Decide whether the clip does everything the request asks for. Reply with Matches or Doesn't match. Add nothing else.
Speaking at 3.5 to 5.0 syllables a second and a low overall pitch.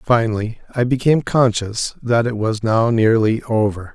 Matches